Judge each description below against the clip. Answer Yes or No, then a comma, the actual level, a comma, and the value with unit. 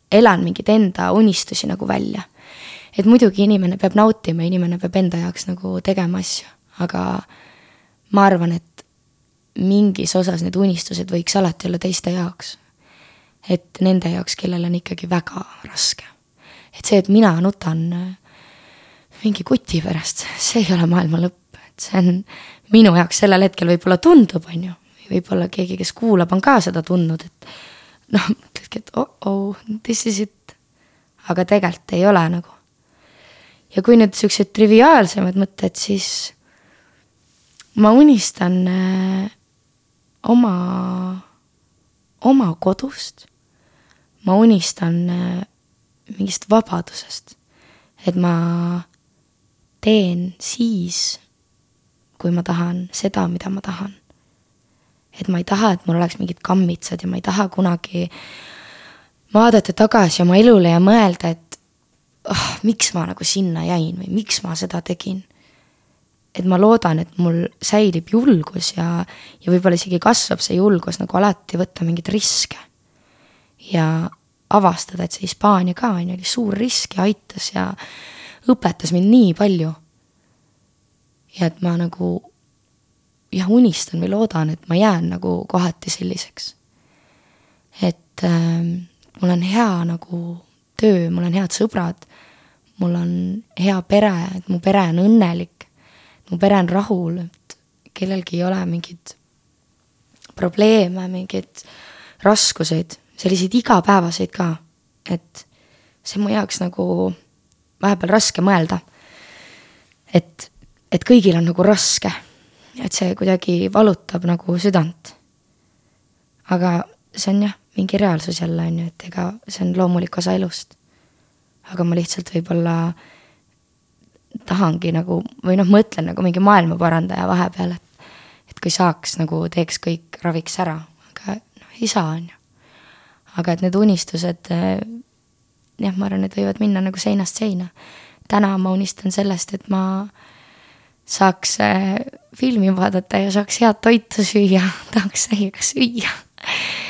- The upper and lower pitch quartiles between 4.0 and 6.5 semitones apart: No, average, 2.9 semitones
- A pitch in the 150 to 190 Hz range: Yes, medium, 185 Hz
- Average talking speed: No, slow, 130 wpm